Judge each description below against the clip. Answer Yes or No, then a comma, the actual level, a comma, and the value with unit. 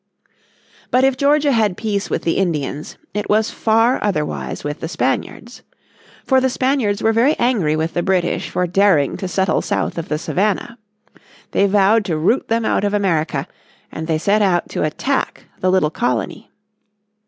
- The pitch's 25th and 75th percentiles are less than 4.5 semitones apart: No, wide, 5.4 semitones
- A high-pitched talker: Yes, high, 200 Hz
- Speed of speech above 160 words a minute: Yes, average, 170 wpm